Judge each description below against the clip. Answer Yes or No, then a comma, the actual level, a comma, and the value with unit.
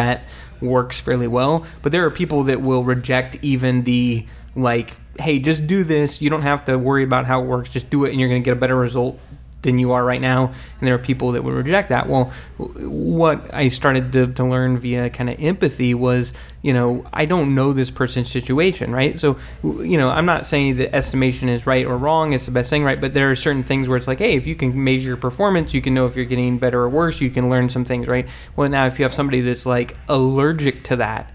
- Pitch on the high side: No, low, 130 Hz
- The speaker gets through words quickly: Yes, fast, 250 wpm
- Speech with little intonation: Yes, narrow, 1.7 semitones